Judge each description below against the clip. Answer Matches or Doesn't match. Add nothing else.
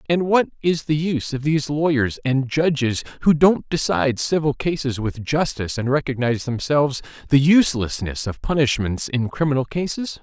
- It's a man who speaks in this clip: Matches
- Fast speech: Doesn't match